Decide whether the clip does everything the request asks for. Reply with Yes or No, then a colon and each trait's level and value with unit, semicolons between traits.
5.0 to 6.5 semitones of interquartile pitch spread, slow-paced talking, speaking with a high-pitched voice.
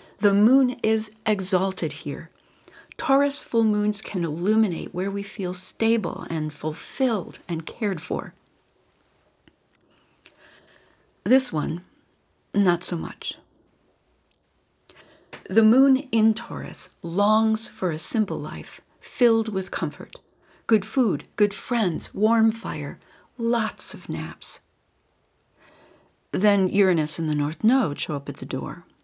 No: average, 4.4 semitones; slow, 115 wpm; high, 210 Hz